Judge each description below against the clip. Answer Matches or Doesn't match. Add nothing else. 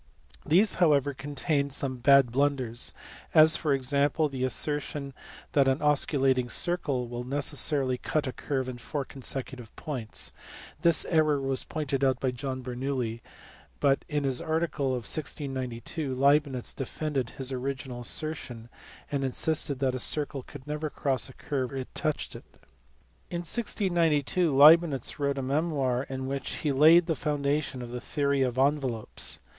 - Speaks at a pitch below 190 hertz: Matches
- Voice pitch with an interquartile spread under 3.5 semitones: Matches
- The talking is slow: Doesn't match